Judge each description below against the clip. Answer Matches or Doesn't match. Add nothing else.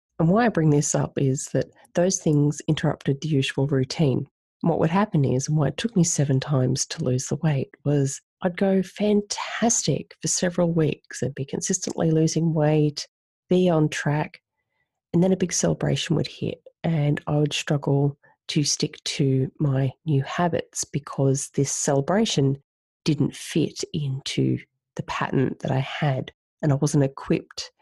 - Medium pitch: Matches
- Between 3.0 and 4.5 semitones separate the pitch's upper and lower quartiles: Matches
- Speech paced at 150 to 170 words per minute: Matches